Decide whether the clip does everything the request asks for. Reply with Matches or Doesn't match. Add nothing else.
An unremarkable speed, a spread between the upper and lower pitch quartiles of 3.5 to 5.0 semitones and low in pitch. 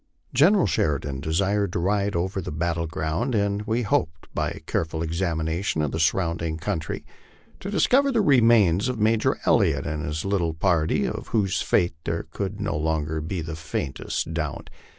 Matches